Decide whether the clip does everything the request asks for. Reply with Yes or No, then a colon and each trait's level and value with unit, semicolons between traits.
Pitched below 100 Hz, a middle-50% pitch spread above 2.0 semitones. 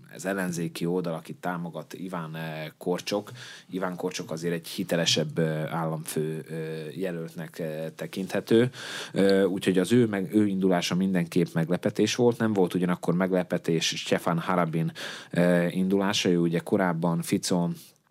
Yes: very low, 90 Hz; narrow, 2.6 semitones